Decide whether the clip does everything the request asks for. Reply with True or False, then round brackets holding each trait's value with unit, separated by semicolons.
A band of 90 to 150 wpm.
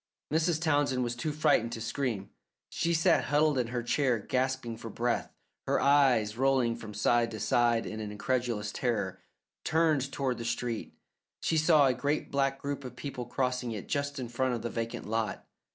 False (180 wpm)